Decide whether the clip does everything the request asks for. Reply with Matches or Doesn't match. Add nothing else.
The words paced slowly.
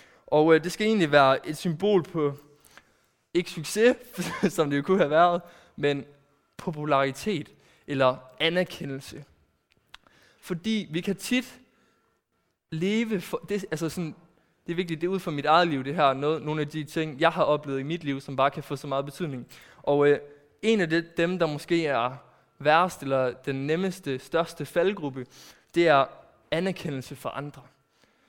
Doesn't match